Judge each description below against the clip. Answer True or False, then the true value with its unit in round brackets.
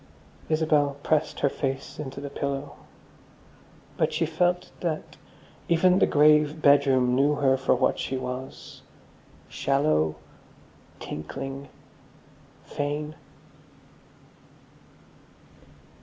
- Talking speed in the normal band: False (90 wpm)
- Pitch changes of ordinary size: False (2.2 semitones)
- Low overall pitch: False (145 Hz)